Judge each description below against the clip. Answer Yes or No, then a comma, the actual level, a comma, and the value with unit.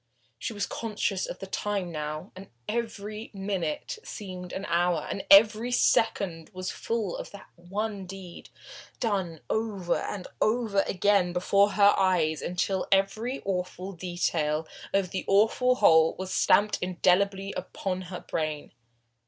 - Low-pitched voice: No, high, 195 Hz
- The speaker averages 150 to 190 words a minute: No, slow, 135 wpm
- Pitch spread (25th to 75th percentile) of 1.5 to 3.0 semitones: Yes, narrow, 2.6 semitones